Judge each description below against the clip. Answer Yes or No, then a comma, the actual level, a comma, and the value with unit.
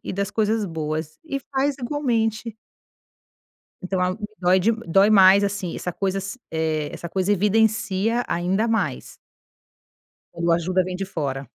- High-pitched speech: Yes, high, 195 Hz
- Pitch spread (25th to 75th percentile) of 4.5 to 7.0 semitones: No, average, 3.9 semitones